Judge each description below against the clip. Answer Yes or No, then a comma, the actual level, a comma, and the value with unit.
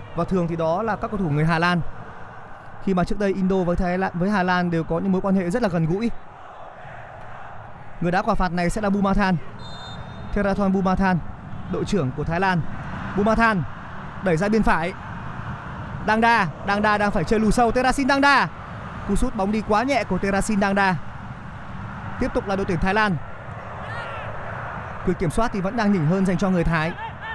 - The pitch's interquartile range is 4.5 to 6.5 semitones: No, average, 3.6 semitones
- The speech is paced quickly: No, average, 205 wpm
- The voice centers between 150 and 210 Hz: Yes, high, 190 Hz